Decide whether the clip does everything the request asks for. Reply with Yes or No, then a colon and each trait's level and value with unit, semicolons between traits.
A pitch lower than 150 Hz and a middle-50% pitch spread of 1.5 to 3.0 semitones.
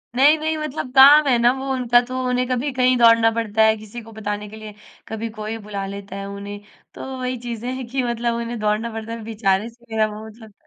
No: high, 230 Hz; average, 2.7 semitones